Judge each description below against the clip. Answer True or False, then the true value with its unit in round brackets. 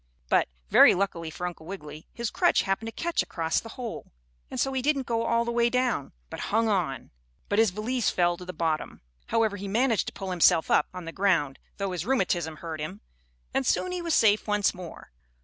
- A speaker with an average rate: False (215 wpm)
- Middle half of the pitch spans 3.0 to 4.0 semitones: False (5.3 semitones)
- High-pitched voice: True (200 Hz)